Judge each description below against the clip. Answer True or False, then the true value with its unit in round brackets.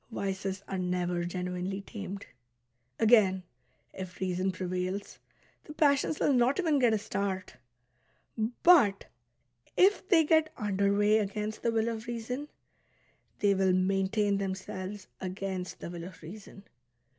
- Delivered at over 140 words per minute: False (135 wpm)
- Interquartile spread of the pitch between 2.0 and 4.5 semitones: True (3.4 semitones)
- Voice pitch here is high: True (200 Hz)